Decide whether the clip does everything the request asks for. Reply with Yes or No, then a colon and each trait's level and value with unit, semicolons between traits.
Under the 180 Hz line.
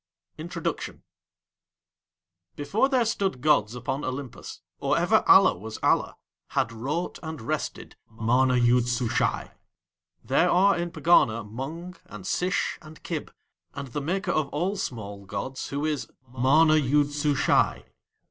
Yes: medium, 140 Hz